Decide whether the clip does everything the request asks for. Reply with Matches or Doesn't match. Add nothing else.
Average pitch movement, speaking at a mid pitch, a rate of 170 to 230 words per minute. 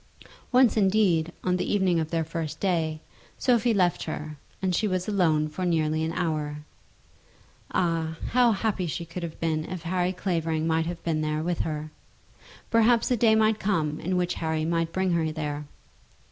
Matches